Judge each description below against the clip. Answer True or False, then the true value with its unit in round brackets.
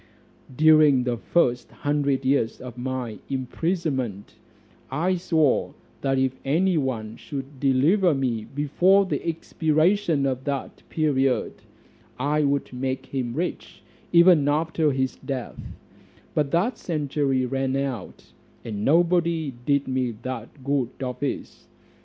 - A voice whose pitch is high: False (140 Hz)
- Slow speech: True (120 wpm)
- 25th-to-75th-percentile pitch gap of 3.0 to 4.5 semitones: True (3.4 semitones)